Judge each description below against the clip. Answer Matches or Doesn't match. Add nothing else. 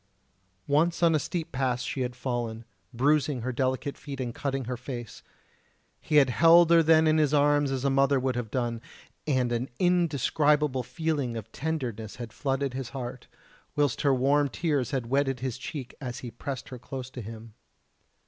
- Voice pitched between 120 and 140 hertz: Matches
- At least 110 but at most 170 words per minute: Doesn't match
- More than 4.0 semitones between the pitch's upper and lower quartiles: Doesn't match